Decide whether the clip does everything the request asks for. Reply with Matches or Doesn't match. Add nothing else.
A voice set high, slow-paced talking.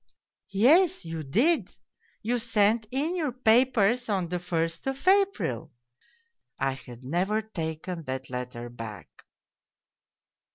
Matches